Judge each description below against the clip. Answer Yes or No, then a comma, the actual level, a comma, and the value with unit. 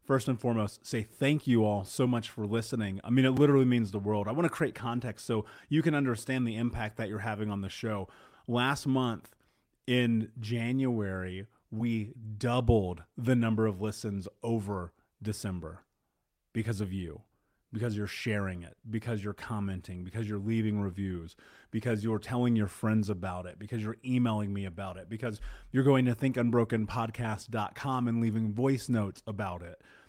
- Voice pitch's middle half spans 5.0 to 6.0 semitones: No, average, 2.8 semitones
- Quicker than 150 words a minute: Yes, average, 170 wpm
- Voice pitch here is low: Yes, low, 110 Hz